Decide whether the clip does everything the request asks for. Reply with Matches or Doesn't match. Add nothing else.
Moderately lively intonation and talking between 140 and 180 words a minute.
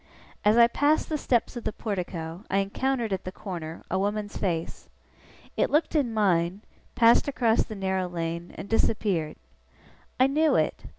Matches